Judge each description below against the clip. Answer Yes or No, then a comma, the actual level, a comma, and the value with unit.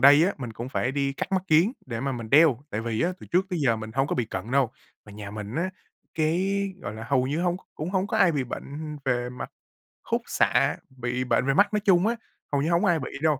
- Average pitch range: No, wide, 5.8 semitones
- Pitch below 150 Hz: Yes, medium, 140 Hz